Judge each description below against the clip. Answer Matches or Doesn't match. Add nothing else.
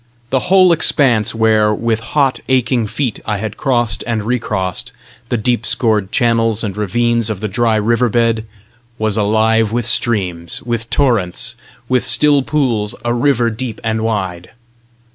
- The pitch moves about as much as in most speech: Doesn't match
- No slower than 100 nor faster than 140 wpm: Doesn't match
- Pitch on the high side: Doesn't match